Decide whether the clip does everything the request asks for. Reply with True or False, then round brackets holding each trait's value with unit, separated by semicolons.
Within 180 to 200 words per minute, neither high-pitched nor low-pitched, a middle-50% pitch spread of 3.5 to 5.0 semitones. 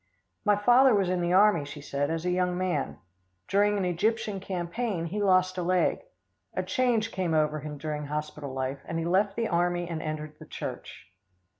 True (190 wpm; 180 Hz; 4.6 semitones)